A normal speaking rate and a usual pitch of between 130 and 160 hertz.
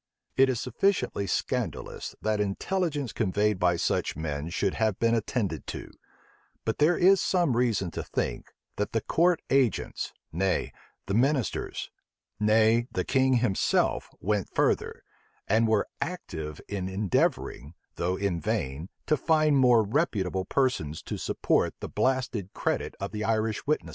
No: average, 145 wpm; low, 110 Hz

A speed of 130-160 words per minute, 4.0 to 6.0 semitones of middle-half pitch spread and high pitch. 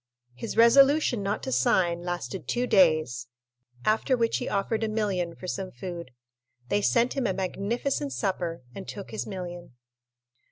Yes: average, 155 wpm; average, 4.7 semitones; high, 195 Hz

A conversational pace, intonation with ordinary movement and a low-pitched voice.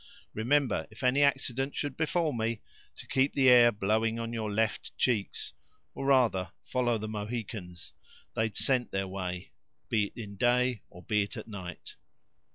Yes: average, 160 wpm; average, 3.8 semitones; low, 115 Hz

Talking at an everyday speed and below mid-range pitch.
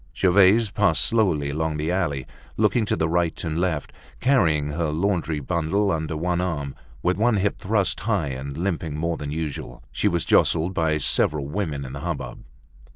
Yes: average, 175 wpm; very low, 85 Hz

